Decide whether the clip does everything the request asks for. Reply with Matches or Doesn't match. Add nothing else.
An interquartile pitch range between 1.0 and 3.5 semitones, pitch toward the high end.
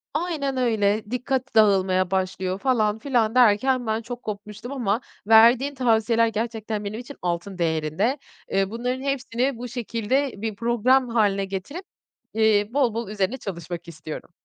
Doesn't match